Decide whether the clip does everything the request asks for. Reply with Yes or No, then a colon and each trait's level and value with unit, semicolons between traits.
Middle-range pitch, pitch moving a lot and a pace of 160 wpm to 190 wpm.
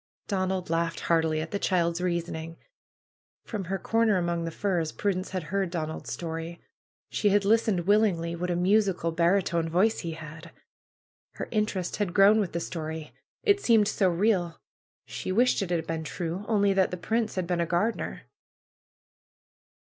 No: medium, 180 Hz; average, 3.3 semitones; average, 165 wpm